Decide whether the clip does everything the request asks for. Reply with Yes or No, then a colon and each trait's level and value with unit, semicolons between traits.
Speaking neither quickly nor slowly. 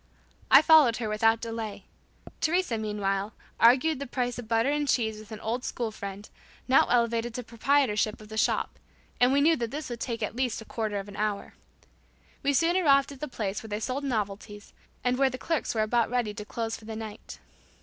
No: fast, 210 wpm